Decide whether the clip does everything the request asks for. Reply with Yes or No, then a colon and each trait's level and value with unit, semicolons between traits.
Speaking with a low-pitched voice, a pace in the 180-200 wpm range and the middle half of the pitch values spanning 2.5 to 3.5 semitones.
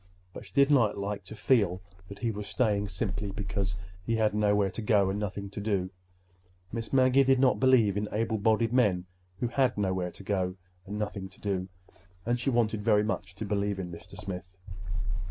Yes: low, 105 Hz; average, 190 wpm; average, 3.0 semitones